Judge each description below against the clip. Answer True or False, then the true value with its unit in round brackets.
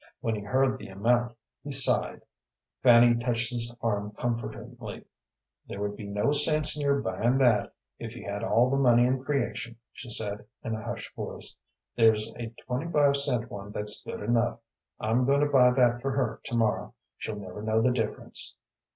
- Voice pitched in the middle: False (120 Hz)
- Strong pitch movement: False (3.2 semitones)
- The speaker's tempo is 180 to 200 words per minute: True (185 wpm)